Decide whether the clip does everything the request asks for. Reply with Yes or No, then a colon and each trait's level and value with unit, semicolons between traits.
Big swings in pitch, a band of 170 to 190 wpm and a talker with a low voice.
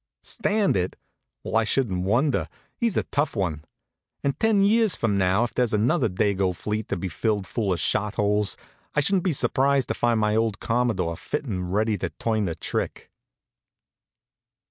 Yes: wide, 6.0 semitones; average, 175 wpm; low, 110 Hz